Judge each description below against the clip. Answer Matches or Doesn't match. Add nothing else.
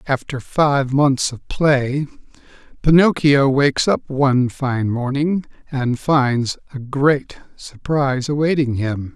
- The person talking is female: Doesn't match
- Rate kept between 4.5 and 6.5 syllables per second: Doesn't match